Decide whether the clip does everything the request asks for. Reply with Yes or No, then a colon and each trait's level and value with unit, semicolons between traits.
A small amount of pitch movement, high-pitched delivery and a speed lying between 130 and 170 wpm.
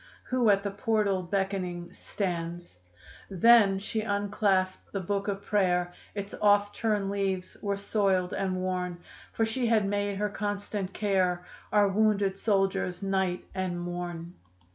Yes: narrow, 1.9 semitones; high, 195 Hz; average, 140 wpm